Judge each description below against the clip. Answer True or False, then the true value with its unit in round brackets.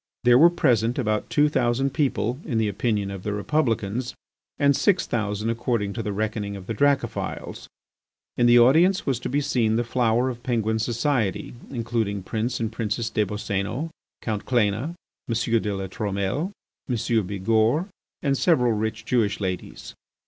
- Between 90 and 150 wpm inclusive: False (160 wpm)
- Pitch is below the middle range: True (115 Hz)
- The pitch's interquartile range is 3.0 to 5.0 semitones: True (3.4 semitones)